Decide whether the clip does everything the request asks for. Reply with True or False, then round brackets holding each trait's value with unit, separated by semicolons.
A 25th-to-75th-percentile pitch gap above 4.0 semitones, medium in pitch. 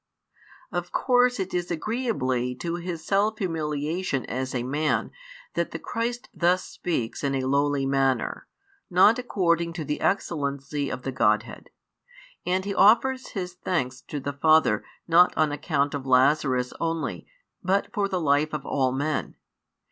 True (5.1 semitones; 155 Hz)